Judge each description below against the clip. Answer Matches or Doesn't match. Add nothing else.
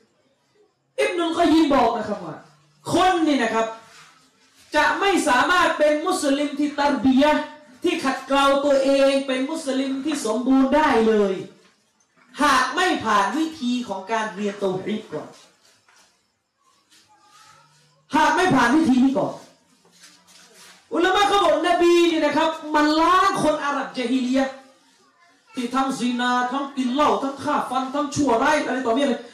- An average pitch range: Matches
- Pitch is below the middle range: Doesn't match